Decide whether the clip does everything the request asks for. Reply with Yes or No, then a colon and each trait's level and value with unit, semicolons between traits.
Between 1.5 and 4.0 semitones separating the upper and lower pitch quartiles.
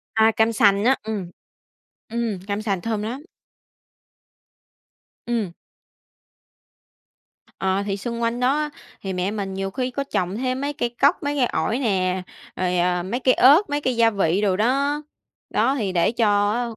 No: average, 4.6 semitones